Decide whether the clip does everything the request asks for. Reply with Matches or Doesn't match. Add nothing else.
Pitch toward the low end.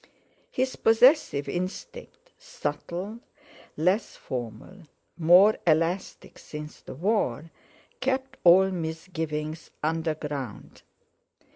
Doesn't match